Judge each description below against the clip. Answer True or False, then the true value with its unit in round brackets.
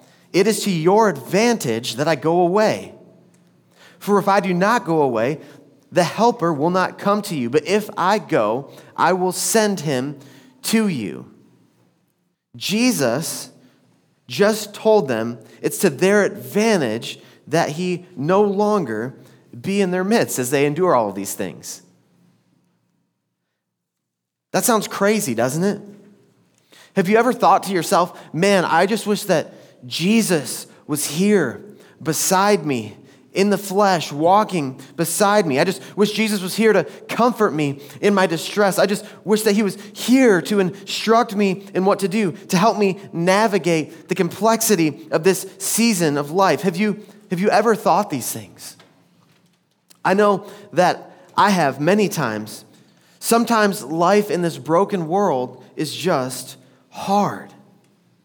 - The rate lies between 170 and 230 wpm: False (150 wpm)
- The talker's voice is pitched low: False (190 Hz)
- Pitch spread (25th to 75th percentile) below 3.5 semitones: False (4.3 semitones)